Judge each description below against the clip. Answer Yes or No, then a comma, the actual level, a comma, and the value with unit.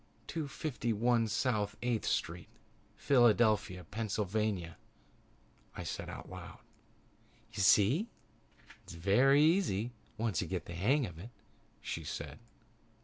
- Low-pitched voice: Yes, low, 110 Hz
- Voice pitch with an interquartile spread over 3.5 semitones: Yes, average, 4.5 semitones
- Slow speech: Yes, slow, 115 wpm